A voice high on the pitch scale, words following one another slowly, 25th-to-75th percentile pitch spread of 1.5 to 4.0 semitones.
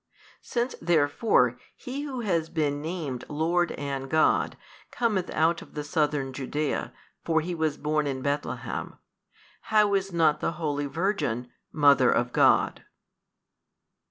No: medium, 155 Hz; slow, 130 wpm; average, 3.6 semitones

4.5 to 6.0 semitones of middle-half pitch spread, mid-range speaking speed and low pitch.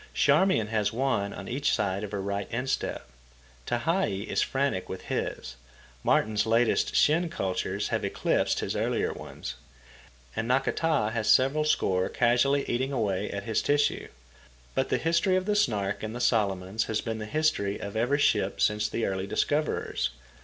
Yes: wide, 5.6 semitones; average, 160 wpm; low, 115 Hz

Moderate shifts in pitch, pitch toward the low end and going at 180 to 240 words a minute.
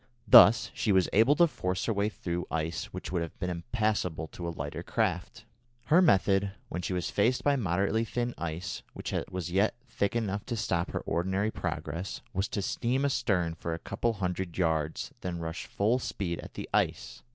Yes: average, 4.4 semitones; very low, 95 Hz; average, 195 wpm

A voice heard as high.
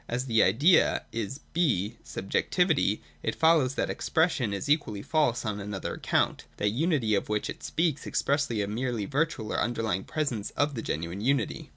No: low, 120 Hz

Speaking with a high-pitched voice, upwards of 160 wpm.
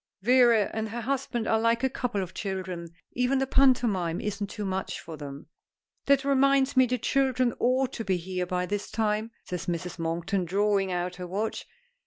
Yes: high, 210 Hz; average, 185 wpm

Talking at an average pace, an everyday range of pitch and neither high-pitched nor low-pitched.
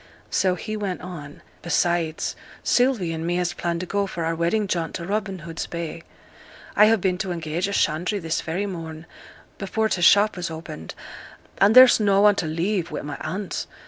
Yes: average, 190 wpm; average, 3.4 semitones; medium, 180 Hz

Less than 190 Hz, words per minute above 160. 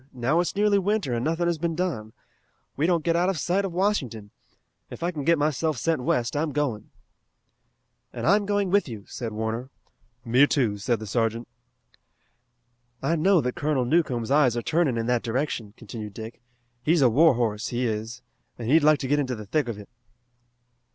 Yes: low, 135 Hz; average, 190 wpm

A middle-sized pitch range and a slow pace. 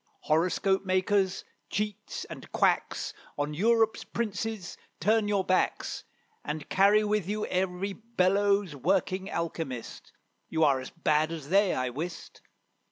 Yes: average, 4.1 semitones; slow, 125 wpm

